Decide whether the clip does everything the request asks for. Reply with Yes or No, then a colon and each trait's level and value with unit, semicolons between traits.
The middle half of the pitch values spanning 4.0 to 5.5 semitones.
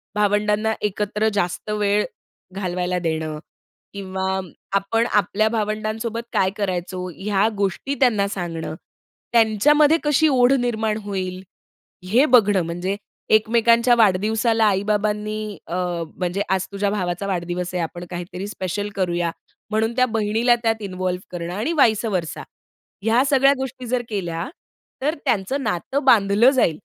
No: average, 3.4 semitones